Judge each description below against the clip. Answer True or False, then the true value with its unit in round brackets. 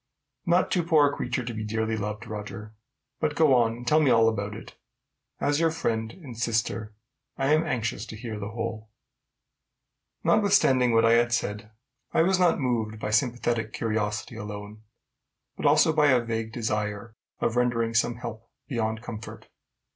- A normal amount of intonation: True (3.0 semitones)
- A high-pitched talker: False (115 Hz)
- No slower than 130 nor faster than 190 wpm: True (170 wpm)